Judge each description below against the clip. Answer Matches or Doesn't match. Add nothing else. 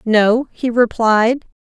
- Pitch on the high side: Matches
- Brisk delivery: Doesn't match